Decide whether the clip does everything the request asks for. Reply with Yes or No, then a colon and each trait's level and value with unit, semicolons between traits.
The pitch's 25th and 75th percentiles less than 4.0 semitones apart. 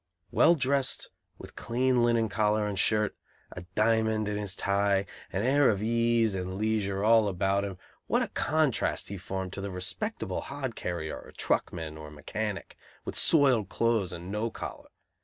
Yes: average, 3.3 semitones